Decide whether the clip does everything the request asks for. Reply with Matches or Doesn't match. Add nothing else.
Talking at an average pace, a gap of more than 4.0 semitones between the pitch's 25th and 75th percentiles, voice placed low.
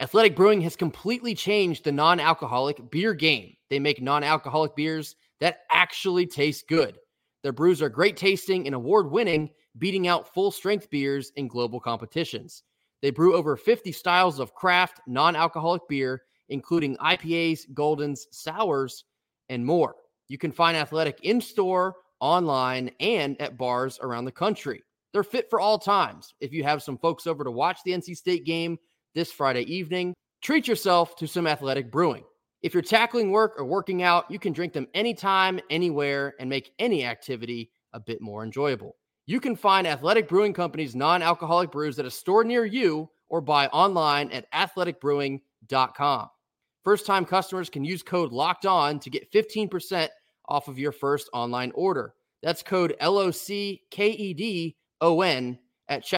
Doesn't match